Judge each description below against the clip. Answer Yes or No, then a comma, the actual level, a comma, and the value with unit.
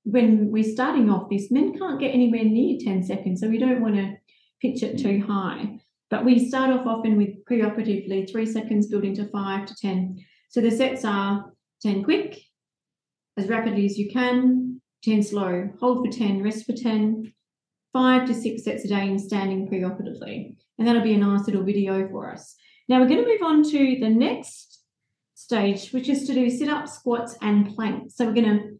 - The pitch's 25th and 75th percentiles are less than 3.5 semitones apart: No, average, 3.8 semitones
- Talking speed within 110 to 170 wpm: No, average, 200 wpm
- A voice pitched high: Yes, high, 225 Hz